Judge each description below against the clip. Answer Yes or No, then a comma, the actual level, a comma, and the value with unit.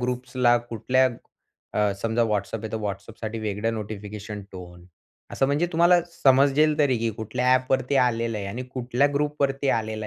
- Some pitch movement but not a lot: Yes, average, 3.8 semitones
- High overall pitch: No, low, 120 Hz